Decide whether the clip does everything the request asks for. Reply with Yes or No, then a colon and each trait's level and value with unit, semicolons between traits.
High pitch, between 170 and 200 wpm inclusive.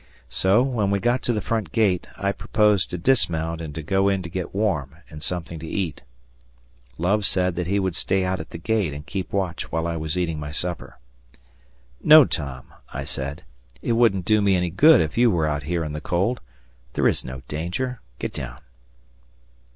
No: very low, 90 Hz; average, 195 wpm